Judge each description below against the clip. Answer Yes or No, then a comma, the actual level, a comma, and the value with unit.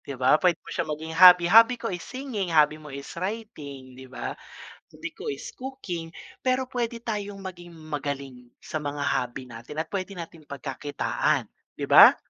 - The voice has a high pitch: No, medium, 165 Hz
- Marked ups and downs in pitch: Yes, wide, 6.9 semitones